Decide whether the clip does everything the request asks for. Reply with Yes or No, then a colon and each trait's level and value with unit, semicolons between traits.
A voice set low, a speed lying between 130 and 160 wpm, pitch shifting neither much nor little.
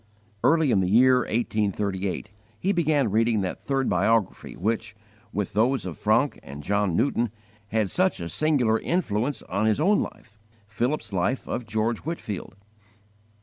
Yes: low, 110 Hz; average, 150 wpm; average, 4.9 semitones